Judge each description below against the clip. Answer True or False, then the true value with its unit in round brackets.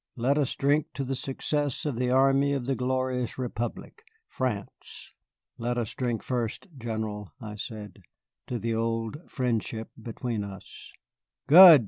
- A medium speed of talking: False (130 wpm)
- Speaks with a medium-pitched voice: False (125 Hz)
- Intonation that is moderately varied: True (3.0 semitones)